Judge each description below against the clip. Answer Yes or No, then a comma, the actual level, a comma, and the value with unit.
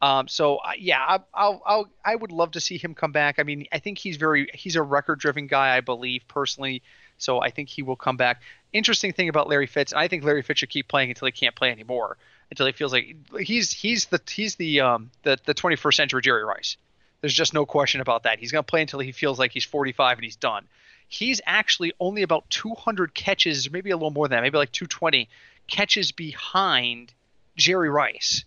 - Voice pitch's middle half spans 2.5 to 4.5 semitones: No, average, 5.1 semitones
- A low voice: No, medium, 150 Hz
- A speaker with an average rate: No, fast, 230 wpm